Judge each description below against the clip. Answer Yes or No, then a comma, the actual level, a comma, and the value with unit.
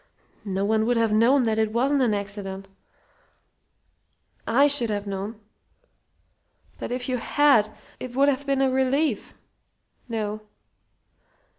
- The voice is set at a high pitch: Yes, high, 230 Hz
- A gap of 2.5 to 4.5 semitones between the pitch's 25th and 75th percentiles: Yes, average, 4.0 semitones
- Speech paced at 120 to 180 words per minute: Yes, average, 140 wpm